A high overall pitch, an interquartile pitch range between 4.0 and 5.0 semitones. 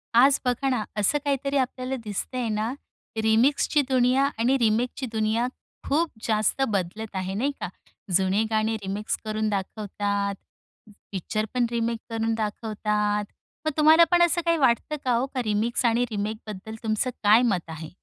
No: high, 225 Hz; average, 3.4 semitones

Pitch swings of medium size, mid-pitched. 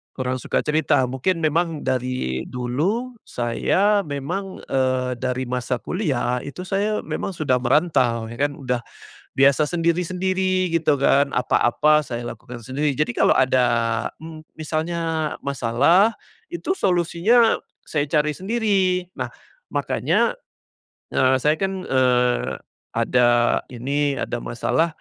No: wide, 5.7 semitones; medium, 145 Hz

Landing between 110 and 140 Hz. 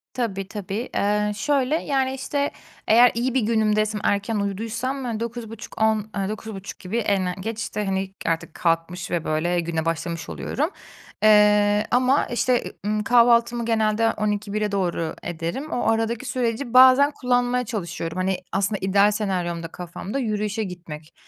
No: high, 210 Hz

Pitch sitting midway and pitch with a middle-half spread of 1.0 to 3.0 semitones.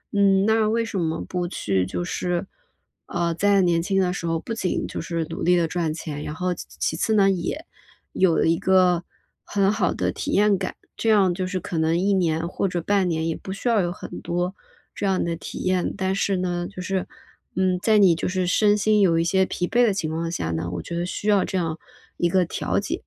Yes: medium, 180 Hz; average, 2.7 semitones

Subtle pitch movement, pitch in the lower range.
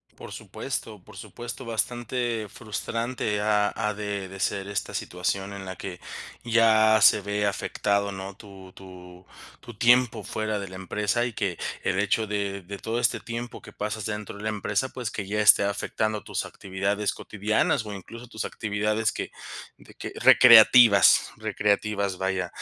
Yes: narrow, 2.1 semitones; low, 105 Hz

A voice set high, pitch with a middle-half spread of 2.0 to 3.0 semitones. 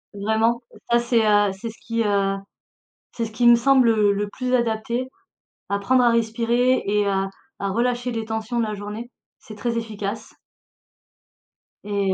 Yes: high, 225 Hz; narrow, 2.5 semitones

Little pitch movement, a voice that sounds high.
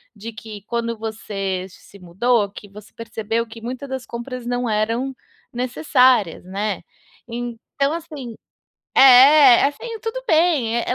No: average, 3.5 semitones; high, 235 Hz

